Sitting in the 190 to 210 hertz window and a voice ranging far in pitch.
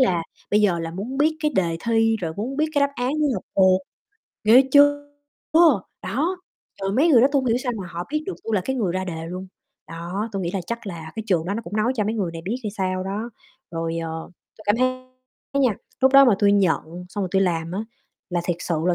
Yes: high, 205 Hz; wide, 5.9 semitones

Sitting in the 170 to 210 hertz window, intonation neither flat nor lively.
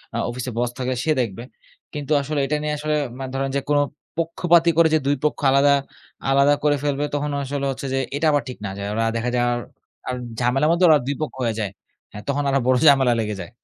No: medium, 140 Hz; average, 3.0 semitones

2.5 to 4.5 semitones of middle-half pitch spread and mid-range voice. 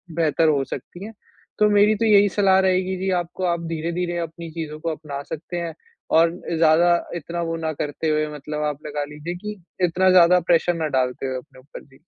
Yes: average, 2.9 semitones; medium, 165 Hz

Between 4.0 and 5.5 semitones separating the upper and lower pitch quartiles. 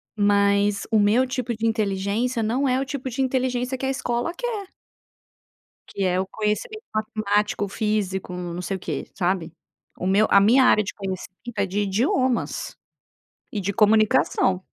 Yes: average, 4.3 semitones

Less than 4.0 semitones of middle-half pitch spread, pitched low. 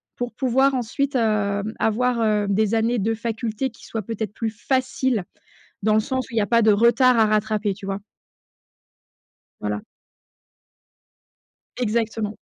No: narrow, 2.4 semitones; high, 225 Hz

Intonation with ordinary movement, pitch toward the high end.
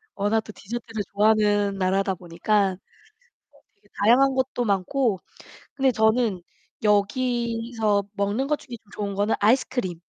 Yes: average, 3.1 semitones; high, 215 Hz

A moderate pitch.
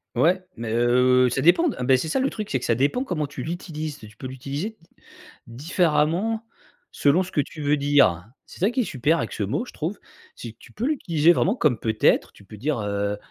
Yes: medium, 145 Hz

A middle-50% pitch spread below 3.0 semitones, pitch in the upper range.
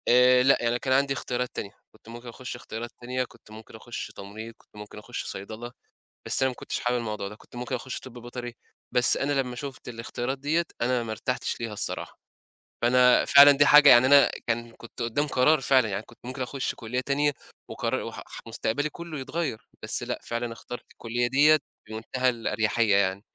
No: narrow, 2.4 semitones; low, 125 Hz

